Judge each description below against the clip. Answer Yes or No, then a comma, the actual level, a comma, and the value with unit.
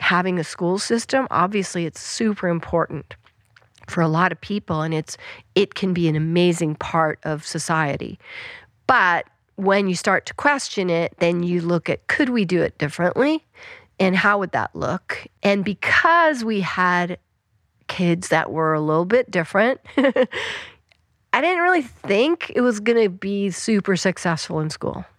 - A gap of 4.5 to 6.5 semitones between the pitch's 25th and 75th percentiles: Yes, average, 5.0 semitones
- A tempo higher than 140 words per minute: Yes, fast, 160 wpm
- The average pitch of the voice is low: No, medium, 180 Hz